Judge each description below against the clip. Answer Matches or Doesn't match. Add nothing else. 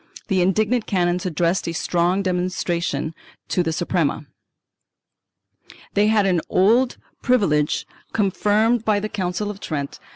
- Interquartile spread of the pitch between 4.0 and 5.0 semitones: Doesn't match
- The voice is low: Doesn't match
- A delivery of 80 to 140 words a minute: Matches